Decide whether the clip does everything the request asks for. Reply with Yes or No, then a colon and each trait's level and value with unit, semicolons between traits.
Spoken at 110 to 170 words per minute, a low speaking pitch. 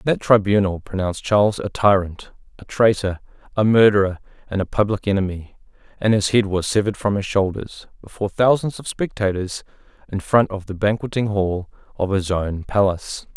Yes: average, 160 wpm; low, 100 Hz